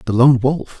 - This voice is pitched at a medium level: No, low, 130 Hz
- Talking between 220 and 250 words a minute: Yes, fast, 225 wpm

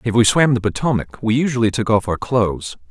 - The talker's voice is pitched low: Yes, low, 115 Hz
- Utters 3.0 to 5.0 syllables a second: No, 5.9 syllables/s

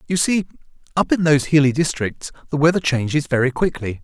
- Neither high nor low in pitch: Yes, medium, 150 Hz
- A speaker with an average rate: Yes, average, 180 wpm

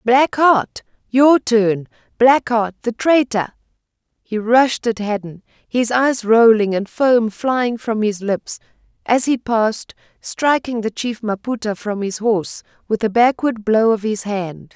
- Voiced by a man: No, female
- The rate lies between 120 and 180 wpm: Yes, average, 155 wpm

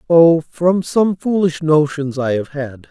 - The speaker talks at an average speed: Yes, average, 165 wpm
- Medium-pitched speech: Yes, medium, 155 Hz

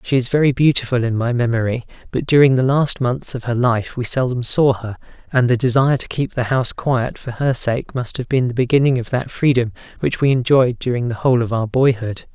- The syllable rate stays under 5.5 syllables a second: No, 5.7 syllables/s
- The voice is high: No, low, 125 Hz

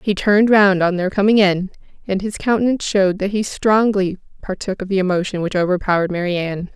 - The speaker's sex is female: Yes, female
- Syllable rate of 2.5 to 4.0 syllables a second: No, 6.1 syllables/s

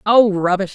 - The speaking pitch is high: Yes, high, 200 Hz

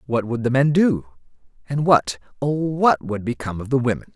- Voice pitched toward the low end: Yes, low, 130 Hz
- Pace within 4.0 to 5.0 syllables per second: No, 5.3 syllables/s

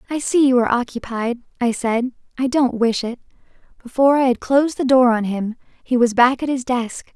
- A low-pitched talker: No, very high, 250 Hz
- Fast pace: Yes, fast, 210 wpm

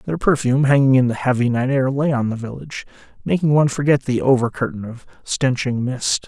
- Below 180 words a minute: No, average, 200 wpm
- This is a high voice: No, low, 130 Hz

